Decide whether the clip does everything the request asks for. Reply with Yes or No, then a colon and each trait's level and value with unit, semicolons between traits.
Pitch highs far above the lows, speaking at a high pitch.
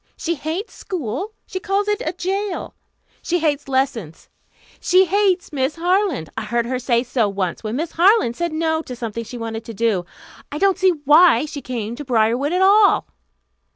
Yes: wide, 7.7 semitones; very high, 295 Hz